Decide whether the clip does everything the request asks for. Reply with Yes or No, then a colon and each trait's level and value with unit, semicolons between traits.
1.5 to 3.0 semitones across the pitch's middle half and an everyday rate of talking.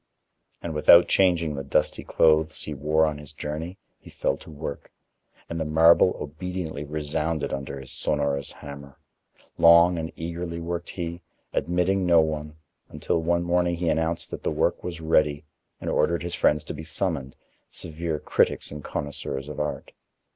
Yes: narrow, 2.4 semitones; average, 160 wpm